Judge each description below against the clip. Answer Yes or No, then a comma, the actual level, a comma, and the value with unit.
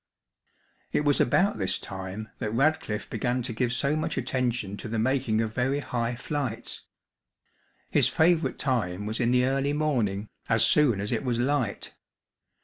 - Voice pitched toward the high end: No, low, 125 Hz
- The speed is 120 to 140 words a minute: No, average, 160 wpm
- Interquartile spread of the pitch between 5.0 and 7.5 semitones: No, average, 3.9 semitones